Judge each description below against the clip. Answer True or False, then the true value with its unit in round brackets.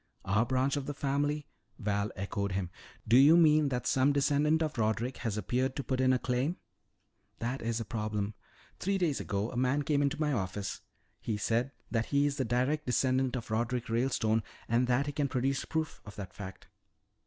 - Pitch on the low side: True (125 Hz)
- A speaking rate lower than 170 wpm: False (195 wpm)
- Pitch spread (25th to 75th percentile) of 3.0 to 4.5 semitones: True (4.1 semitones)